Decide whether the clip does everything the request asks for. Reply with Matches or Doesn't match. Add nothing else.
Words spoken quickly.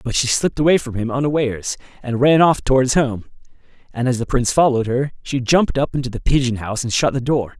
Matches